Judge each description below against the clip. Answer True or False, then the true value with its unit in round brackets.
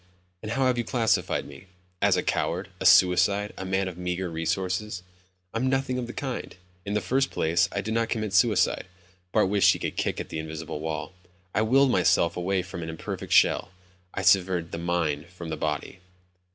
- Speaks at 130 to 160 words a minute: False (195 wpm)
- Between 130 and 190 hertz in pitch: False (95 Hz)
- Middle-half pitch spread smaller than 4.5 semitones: True (4.0 semitones)